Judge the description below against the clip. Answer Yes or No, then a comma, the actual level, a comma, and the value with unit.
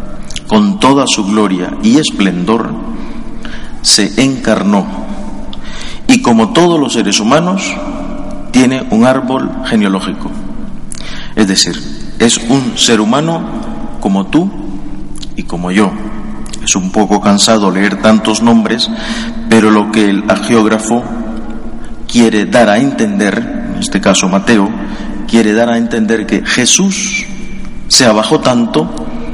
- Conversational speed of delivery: No, slow, 120 wpm